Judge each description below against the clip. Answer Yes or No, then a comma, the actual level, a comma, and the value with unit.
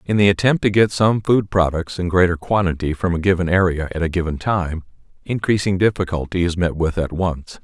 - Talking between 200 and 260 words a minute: Yes, fast, 205 wpm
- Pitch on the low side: Yes, very low, 90 Hz